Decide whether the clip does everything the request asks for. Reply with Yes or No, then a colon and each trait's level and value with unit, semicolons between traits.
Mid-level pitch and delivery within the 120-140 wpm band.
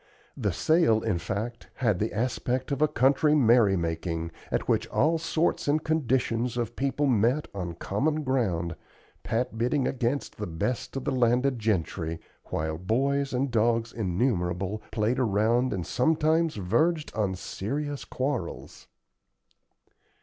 No: low, 120 Hz; slow, 135 wpm